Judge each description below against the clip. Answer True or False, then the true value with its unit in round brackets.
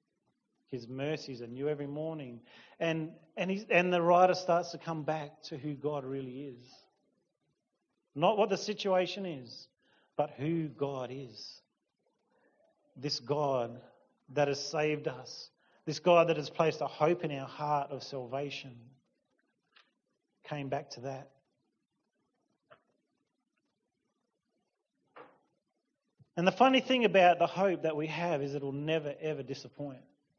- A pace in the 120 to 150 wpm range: True (135 wpm)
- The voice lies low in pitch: False (150 Hz)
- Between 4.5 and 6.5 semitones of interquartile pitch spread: False (3.8 semitones)